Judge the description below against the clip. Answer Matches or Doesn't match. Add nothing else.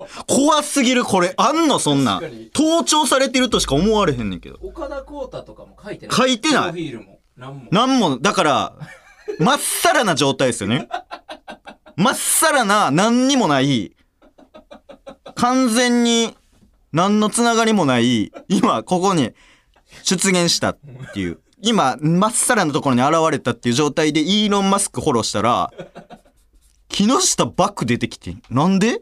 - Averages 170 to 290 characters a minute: Matches